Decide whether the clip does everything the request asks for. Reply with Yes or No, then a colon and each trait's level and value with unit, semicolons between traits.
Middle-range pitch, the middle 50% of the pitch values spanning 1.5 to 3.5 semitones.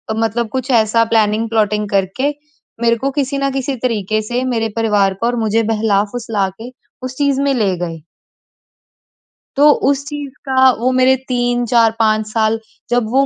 No: high, 230 Hz; average, 3.1 semitones